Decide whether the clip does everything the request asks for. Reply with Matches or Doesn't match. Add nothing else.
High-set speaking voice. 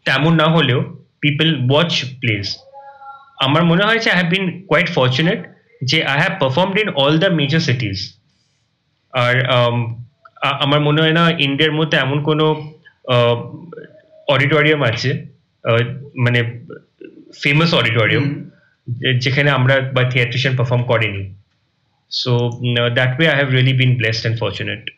Doesn't match